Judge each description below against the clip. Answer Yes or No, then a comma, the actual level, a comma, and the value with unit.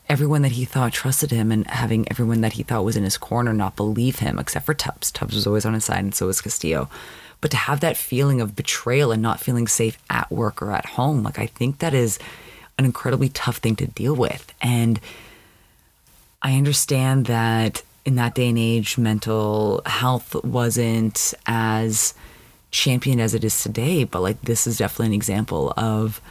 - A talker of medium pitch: No, low, 115 Hz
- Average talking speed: Yes, average, 195 wpm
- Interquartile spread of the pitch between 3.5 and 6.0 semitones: No, average, 2.8 semitones